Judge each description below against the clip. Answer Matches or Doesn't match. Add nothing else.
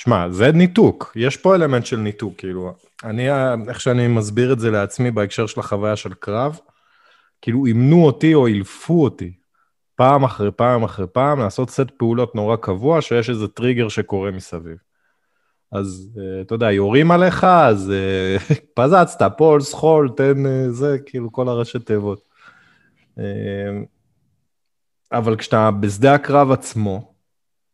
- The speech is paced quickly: Doesn't match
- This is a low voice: Matches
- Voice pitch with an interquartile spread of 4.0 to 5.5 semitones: Matches